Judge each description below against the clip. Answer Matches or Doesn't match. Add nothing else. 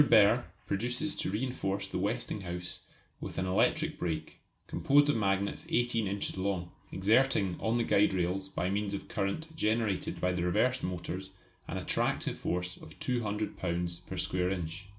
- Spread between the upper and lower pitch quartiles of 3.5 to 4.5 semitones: Matches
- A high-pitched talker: Doesn't match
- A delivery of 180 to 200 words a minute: Doesn't match